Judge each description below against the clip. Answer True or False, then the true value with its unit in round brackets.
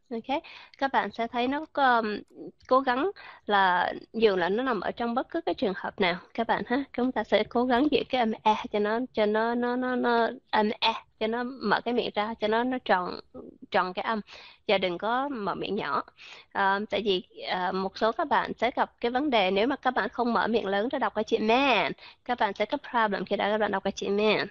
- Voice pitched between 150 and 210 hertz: False (225 Hz)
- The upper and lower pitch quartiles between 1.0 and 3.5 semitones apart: True (3.1 semitones)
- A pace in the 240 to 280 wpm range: True (250 wpm)